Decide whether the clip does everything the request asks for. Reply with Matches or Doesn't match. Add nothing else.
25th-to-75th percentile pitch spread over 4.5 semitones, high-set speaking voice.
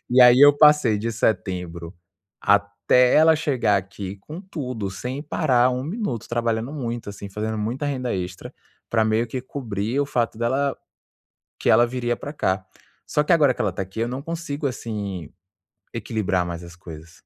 Doesn't match